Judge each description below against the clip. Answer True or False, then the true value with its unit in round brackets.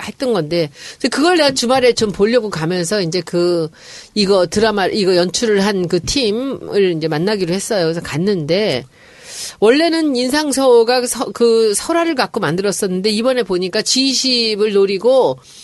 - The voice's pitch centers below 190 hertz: False (215 Hz)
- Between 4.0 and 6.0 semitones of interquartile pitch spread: True (5.5 semitones)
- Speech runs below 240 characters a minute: False (310 characters per minute)